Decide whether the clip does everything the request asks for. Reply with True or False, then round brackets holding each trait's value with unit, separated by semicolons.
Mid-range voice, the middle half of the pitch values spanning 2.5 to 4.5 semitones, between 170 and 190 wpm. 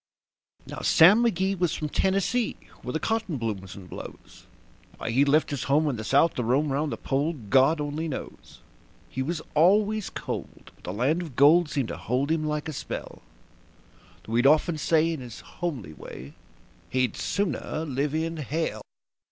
True (150 Hz; 4.2 semitones; 180 wpm)